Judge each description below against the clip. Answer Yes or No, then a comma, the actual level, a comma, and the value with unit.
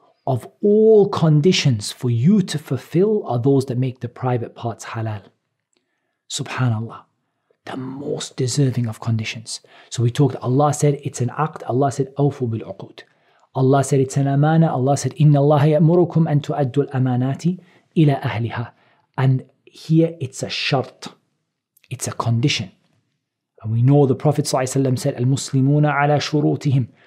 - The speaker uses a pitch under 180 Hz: Yes, medium, 140 Hz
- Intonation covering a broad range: No, average, 3.1 semitones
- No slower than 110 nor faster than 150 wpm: Yes, average, 145 wpm